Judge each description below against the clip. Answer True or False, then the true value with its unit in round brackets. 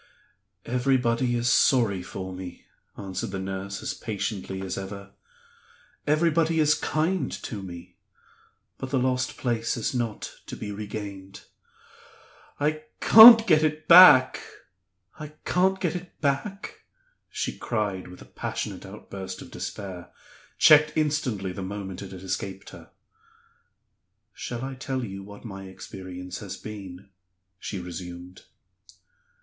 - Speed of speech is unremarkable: False (125 wpm)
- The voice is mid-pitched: False (110 Hz)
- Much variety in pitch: True (7.3 semitones)